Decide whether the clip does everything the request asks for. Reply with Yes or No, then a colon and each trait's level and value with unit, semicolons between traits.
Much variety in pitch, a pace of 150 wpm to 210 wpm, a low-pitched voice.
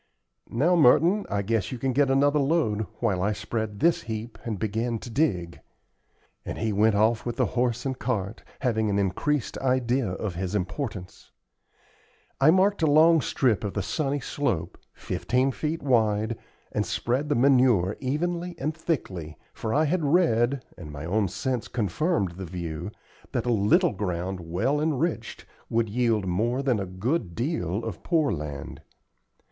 Yes: wide, 5.8 semitones; average, 165 wpm; low, 115 Hz